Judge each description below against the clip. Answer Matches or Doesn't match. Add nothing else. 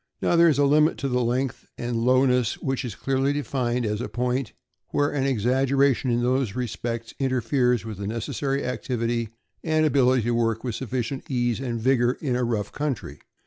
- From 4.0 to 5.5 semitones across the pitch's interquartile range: Doesn't match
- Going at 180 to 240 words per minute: Matches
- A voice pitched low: Matches